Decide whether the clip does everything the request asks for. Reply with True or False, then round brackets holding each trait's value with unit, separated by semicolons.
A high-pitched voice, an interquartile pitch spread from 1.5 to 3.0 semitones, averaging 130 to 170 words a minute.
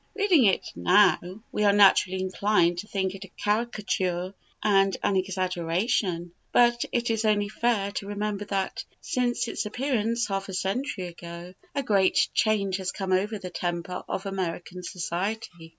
True (195 Hz; 2.7 semitones; 155 wpm)